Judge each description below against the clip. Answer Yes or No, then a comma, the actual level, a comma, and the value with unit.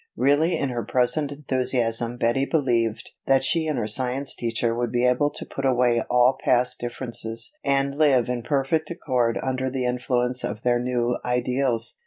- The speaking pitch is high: No, low, 125 Hz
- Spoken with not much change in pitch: Yes, narrow, 2.0 semitones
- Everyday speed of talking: Yes, average, 170 wpm